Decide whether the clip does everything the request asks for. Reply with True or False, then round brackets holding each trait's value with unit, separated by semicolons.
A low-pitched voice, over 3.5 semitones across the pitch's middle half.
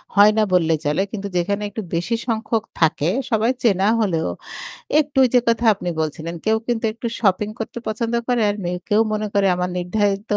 False (205 Hz; 4.0 semitones)